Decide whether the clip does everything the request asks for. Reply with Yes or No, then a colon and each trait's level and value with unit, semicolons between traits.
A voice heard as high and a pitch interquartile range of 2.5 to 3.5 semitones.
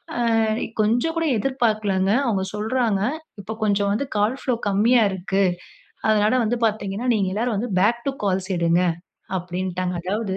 Yes: high, 210 Hz; average, 3.2 semitones